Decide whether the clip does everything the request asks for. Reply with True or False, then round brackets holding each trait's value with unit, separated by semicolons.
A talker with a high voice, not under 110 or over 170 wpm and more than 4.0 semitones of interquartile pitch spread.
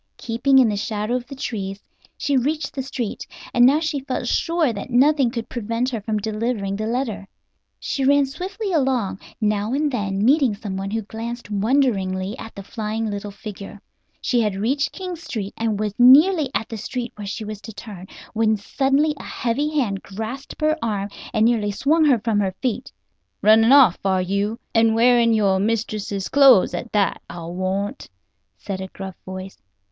False (225 Hz; 180 wpm; 4.6 semitones)